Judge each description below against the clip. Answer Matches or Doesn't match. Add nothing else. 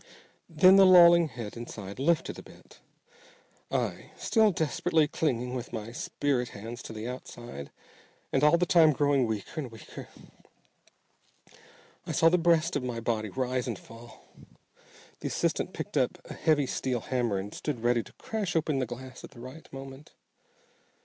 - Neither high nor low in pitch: Doesn't match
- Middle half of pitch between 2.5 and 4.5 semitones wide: Doesn't match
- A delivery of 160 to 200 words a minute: Matches